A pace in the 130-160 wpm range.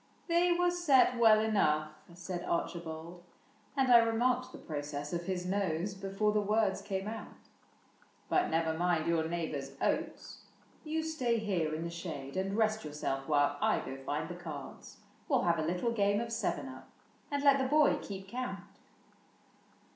No: average, 175 wpm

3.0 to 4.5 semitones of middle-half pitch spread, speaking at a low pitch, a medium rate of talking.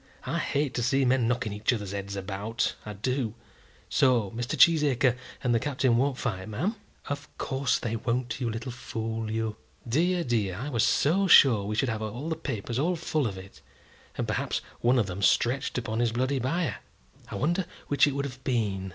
Yes: average, 4.1 semitones; low, 120 Hz; average, 195 wpm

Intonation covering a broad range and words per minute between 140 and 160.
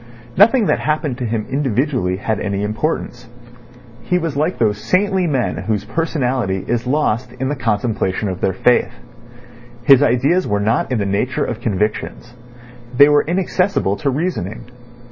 Yes: wide, 5.9 semitones; average, 155 wpm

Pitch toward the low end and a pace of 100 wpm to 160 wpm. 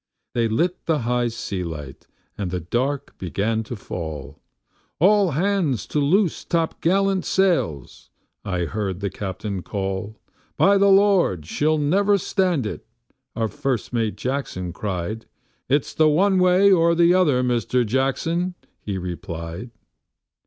Yes: low, 125 Hz; slow, 135 wpm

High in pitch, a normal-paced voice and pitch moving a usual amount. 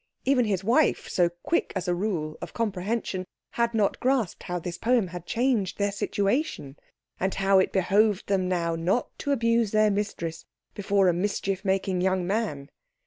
Yes: high, 195 Hz; average, 170 wpm; average, 3.8 semitones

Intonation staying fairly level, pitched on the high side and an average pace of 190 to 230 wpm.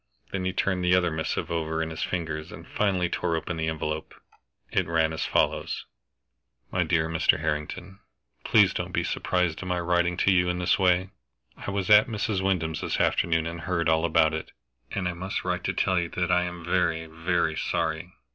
No: narrow, 2.2 semitones; very low, 85 Hz; average, 200 wpm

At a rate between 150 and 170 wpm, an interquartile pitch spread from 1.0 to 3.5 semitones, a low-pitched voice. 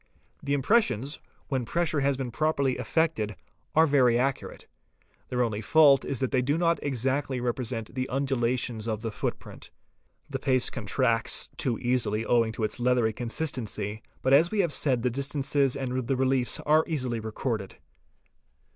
Yes: average, 160 wpm; average, 3.1 semitones; low, 130 Hz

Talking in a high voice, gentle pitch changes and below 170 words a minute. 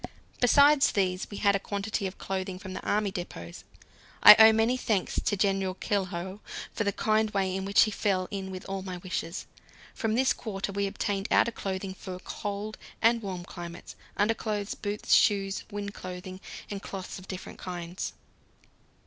No: high, 195 Hz; narrow, 2.1 semitones; average, 175 wpm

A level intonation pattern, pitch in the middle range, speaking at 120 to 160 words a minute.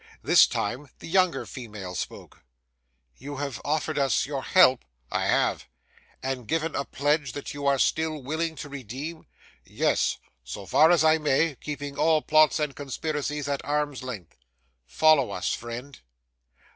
No: average, 3.0 semitones; medium, 145 Hz; average, 150 wpm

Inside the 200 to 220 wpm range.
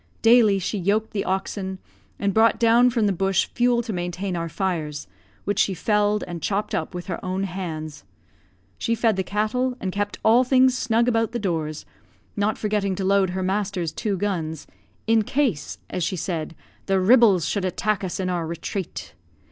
No: average, 180 wpm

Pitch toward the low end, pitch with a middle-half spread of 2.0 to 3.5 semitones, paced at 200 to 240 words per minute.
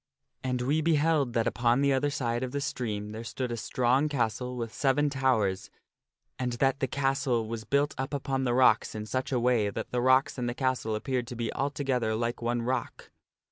Yes: low, 125 Hz; narrow, 2.5 semitones; fast, 205 wpm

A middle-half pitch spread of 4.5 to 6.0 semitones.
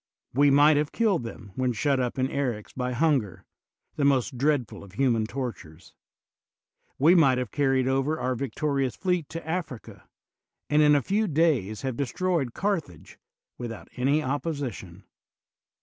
No: average, 3.7 semitones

